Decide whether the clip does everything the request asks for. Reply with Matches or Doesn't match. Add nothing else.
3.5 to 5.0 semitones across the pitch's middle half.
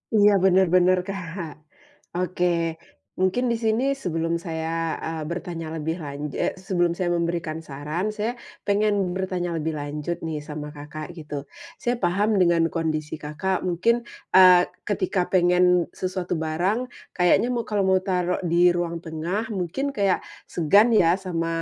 Doesn't match